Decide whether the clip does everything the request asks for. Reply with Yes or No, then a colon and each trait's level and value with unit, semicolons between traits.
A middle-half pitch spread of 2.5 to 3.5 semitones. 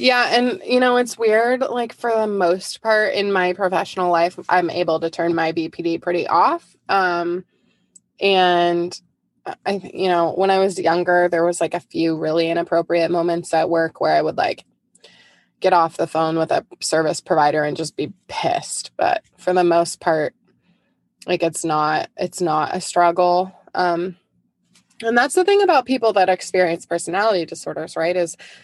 Yes: average, 2.8 semitones